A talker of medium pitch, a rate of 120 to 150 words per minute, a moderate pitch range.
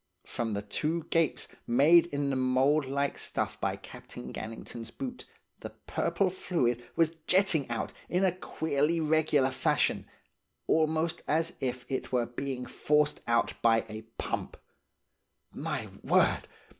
Yes: medium, 145 Hz; slow, 135 wpm; average, 4.7 semitones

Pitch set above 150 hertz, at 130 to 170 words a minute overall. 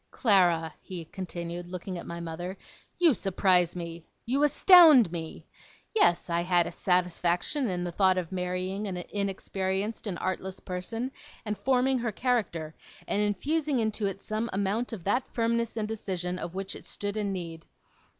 Yes: high, 190 Hz; average, 160 wpm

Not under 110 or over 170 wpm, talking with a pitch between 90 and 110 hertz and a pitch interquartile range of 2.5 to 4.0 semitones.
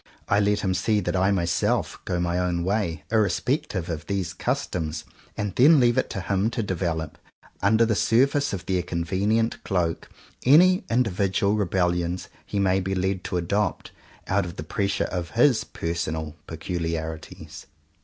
Yes: average, 160 wpm; very low, 95 Hz; average, 3.4 semitones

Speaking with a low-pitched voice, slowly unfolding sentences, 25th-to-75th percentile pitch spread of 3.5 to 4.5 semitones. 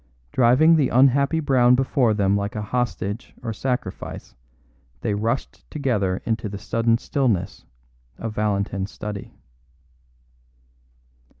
Yes: low, 115 Hz; slow, 110 wpm; average, 4.0 semitones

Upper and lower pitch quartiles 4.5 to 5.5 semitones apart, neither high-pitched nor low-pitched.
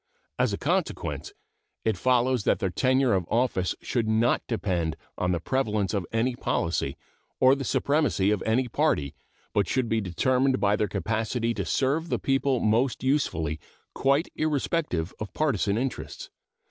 No: average, 4.8 semitones; low, 115 Hz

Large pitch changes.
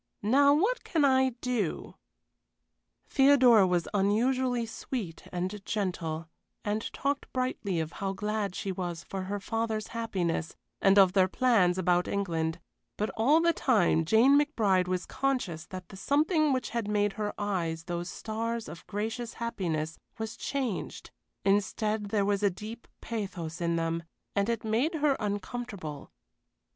No: average, 4.8 semitones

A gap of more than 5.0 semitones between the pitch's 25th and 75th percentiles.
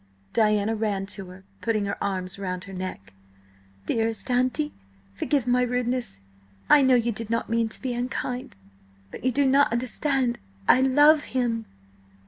No: average, 4.2 semitones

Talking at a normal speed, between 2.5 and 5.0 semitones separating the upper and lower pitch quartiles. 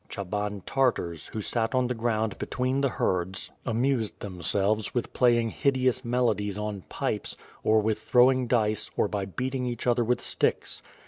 Yes: average, 155 wpm; average, 3.4 semitones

